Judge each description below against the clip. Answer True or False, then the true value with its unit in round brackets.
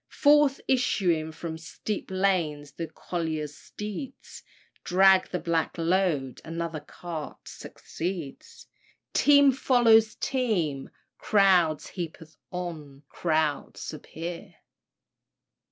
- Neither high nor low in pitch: True (170 Hz)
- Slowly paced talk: True (90 wpm)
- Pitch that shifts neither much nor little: True (3.9 semitones)